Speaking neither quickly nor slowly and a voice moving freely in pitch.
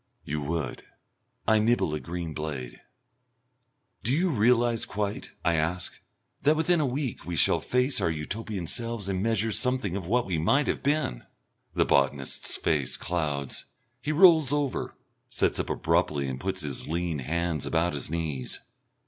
Yes: average, 155 wpm; wide, 7.8 semitones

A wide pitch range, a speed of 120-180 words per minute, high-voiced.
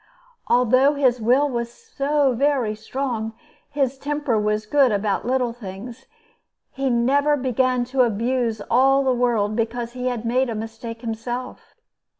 No: average, 2.9 semitones; average, 150 wpm; high, 245 Hz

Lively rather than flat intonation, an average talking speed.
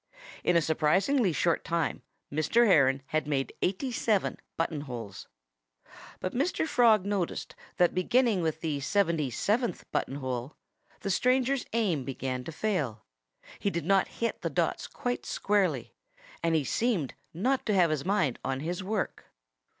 Yes: wide, 6.3 semitones; average, 150 wpm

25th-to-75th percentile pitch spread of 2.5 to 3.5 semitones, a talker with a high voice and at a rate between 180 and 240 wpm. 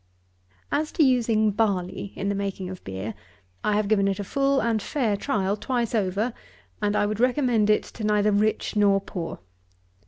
Yes: average, 2.8 semitones; high, 210 Hz; average, 190 wpm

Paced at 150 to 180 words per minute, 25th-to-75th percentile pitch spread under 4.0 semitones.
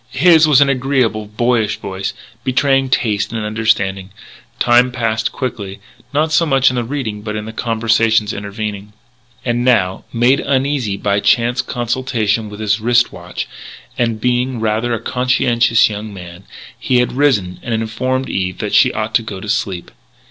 Yes: average, 165 wpm; average, 3.2 semitones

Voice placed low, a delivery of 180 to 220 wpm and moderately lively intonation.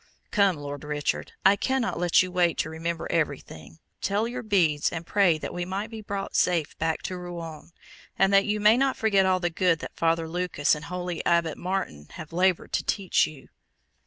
No: medium, 175 Hz; average, 195 wpm; average, 3.5 semitones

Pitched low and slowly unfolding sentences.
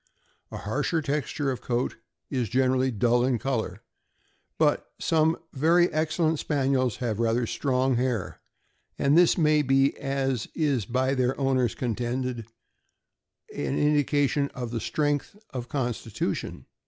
Yes: low, 130 Hz; slow, 125 wpm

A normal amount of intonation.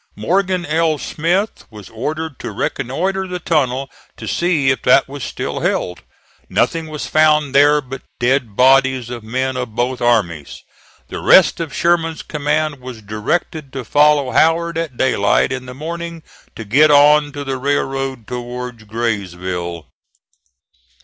Yes: average, 4.3 semitones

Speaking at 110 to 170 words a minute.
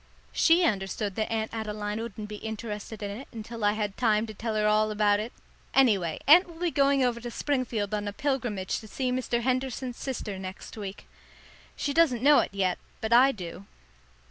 No: average, 195 wpm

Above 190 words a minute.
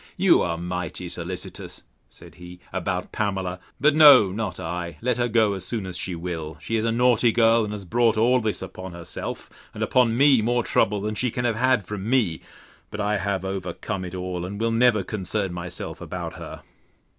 Yes: average, 200 wpm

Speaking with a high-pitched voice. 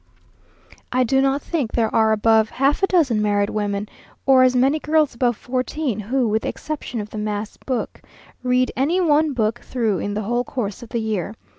Yes: high, 240 Hz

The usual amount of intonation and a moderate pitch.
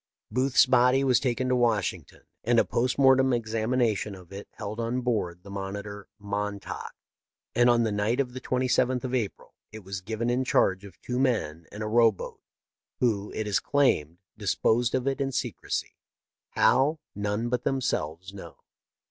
No: average, 3.8 semitones; low, 115 Hz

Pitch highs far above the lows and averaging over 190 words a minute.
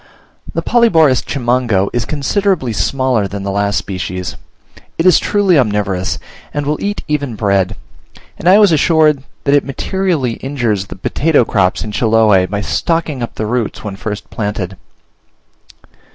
No: wide, 6.9 semitones; average, 150 wpm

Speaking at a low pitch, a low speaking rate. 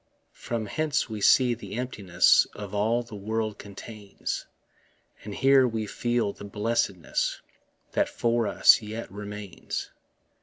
Yes: low, 110 Hz; slow, 125 wpm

